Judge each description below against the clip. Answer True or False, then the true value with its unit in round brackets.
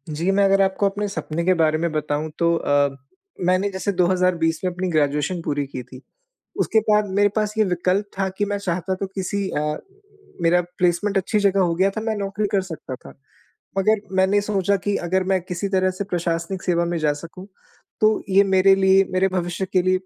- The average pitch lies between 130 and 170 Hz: False (185 Hz)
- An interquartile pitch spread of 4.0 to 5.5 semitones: False (2.7 semitones)